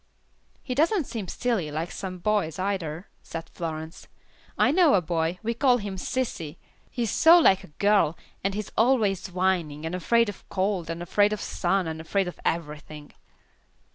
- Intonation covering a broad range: No, average, 4.6 semitones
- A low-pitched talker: No, high, 190 Hz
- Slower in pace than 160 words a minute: No, average, 175 wpm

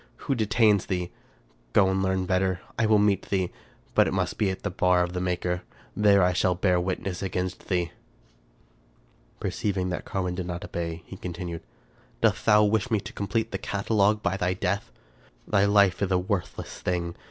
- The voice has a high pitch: No, very low, 95 Hz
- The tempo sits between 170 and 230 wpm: Yes, average, 185 wpm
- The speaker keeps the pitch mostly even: Yes, narrow, 2.1 semitones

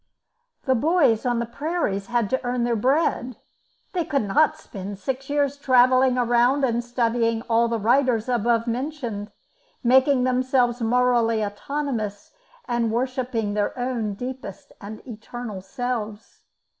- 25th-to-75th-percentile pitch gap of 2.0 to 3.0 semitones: Yes, narrow, 2.5 semitones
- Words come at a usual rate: No, slow, 130 wpm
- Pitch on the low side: No, high, 240 Hz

